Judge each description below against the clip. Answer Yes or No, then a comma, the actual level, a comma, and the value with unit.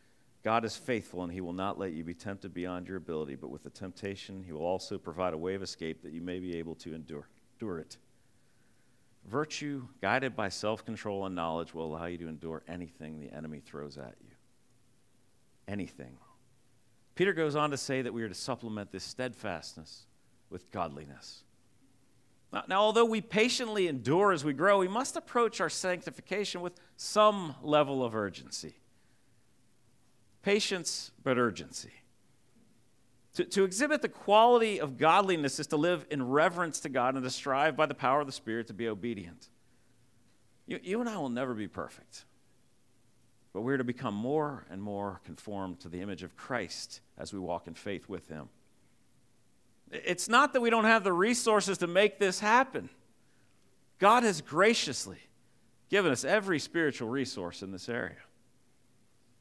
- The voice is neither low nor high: No, low, 120 Hz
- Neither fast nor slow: Yes, average, 170 wpm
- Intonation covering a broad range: Yes, wide, 8.2 semitones